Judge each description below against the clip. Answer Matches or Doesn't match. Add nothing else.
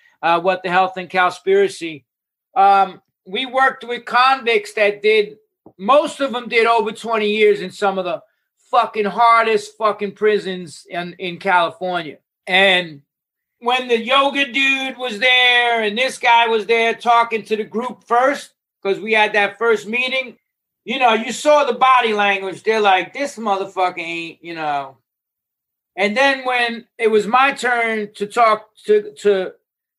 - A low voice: Doesn't match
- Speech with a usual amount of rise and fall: Matches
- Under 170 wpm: Matches